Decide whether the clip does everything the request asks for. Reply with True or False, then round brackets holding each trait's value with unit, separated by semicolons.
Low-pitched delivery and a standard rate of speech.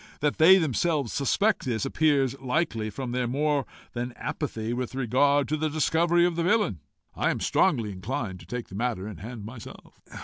True (130 Hz; 180 wpm)